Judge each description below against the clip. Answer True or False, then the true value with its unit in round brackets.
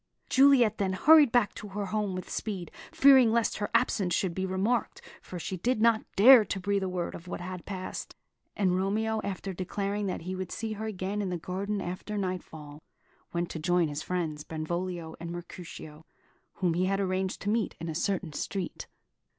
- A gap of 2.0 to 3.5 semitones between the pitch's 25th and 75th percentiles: True (3.0 semitones)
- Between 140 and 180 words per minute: False (190 wpm)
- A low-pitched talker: False (190 Hz)